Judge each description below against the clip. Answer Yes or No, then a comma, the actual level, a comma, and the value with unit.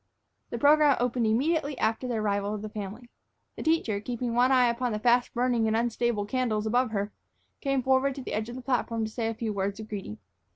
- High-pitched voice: Yes, high, 235 Hz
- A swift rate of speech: Yes, fast, 220 wpm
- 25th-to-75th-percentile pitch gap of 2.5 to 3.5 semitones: Yes, average, 2.8 semitones